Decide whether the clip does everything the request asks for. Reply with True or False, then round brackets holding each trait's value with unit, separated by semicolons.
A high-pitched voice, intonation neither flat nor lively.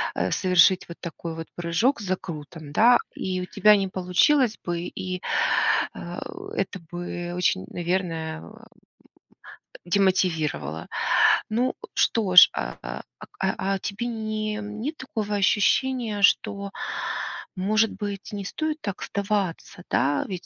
True (195 Hz; 3.4 semitones)